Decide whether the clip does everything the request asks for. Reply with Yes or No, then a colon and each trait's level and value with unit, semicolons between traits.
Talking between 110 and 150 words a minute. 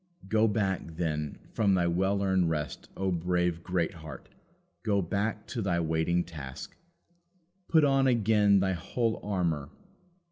Yes: slow, 135 wpm